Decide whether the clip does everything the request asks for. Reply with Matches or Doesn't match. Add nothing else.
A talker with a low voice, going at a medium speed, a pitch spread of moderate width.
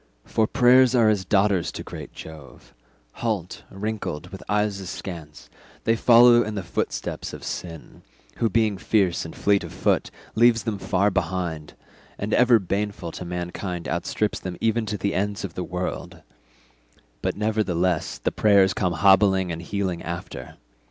Matches